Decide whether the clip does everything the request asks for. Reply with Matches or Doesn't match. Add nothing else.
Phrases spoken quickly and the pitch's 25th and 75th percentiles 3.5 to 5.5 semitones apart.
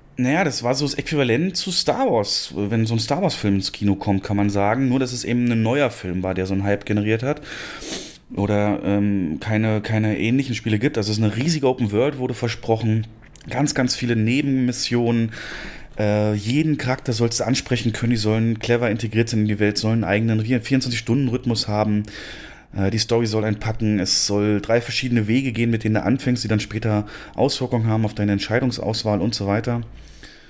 Doesn't match